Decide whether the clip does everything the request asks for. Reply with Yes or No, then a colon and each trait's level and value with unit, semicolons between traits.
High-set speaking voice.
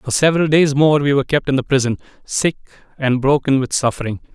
No: medium, 140 Hz